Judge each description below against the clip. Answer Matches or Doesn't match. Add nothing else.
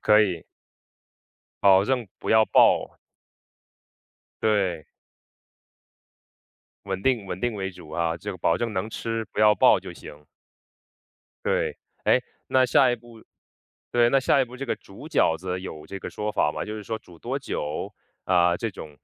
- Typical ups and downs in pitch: Matches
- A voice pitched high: Doesn't match